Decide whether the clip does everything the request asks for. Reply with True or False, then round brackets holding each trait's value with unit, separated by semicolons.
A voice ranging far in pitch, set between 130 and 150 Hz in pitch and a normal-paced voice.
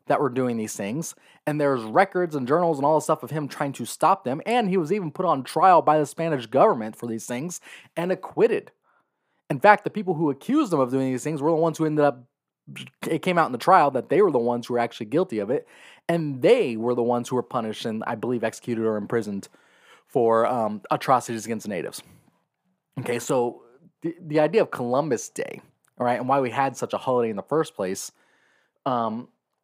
False (5.7 semitones; 135 Hz; 225 wpm)